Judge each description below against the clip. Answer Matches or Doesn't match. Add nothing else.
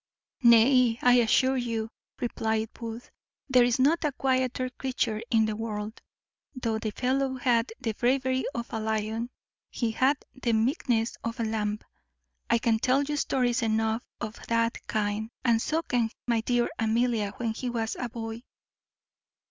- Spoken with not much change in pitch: Matches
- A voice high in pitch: Matches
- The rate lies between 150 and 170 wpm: Matches